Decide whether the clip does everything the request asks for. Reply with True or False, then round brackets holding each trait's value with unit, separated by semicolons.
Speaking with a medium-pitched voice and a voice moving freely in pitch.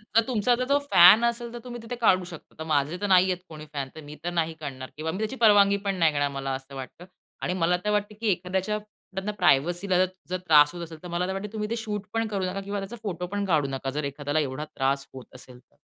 True (180 Hz; 5.7 semitones)